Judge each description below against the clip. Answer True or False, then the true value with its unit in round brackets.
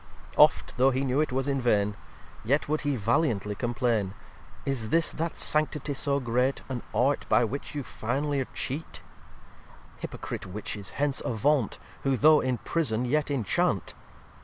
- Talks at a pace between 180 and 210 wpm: False (155 wpm)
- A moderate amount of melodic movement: True (3.7 semitones)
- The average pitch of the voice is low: True (130 Hz)